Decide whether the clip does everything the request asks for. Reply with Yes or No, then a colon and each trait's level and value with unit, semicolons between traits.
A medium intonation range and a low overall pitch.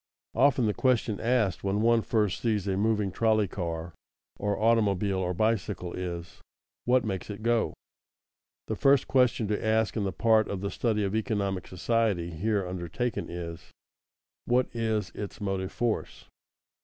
Yes: average, 3.3 semitones; low, 105 Hz